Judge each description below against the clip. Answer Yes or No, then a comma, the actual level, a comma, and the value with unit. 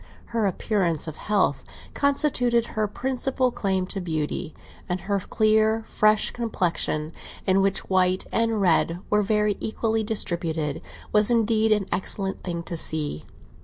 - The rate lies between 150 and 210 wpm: No, slow, 135 wpm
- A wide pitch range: No, average, 3.9 semitones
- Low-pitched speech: No, high, 205 Hz